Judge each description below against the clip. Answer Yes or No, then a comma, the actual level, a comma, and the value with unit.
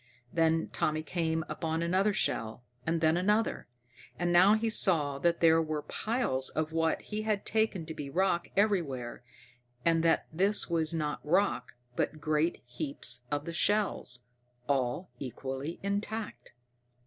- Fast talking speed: No, average, 145 wpm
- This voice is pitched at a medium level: Yes, medium, 165 Hz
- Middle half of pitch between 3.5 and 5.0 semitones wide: Yes, average, 4.3 semitones